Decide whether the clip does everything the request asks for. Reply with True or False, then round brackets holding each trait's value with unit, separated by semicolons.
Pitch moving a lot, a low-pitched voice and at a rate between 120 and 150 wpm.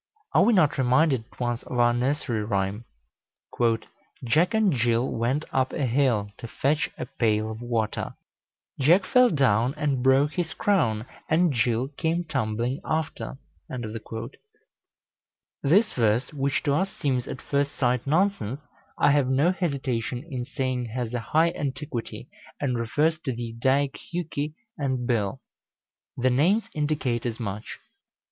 False (4.3 semitones; 130 Hz; 145 wpm)